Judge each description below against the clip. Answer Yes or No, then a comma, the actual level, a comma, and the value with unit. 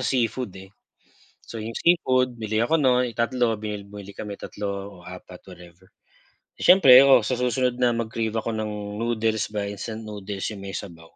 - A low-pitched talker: Yes, low, 110 Hz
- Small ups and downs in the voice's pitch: No, average, 3.4 semitones